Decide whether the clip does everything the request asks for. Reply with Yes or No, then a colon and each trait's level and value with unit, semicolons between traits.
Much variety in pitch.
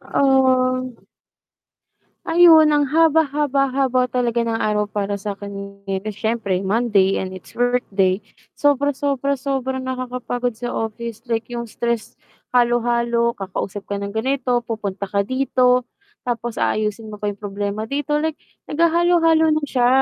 No: average, 4.3 semitones